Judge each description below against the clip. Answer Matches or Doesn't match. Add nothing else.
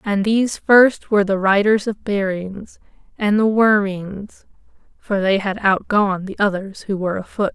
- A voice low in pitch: Doesn't match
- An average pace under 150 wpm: Doesn't match